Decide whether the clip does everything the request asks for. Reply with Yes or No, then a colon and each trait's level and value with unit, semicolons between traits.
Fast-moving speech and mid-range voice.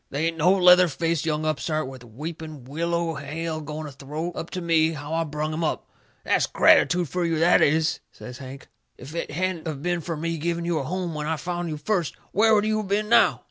Yes: fast, 230 wpm; medium, 160 Hz